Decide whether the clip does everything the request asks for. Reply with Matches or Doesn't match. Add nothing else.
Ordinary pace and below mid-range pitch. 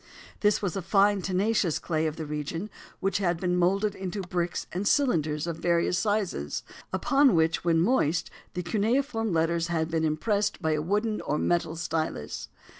Doesn't match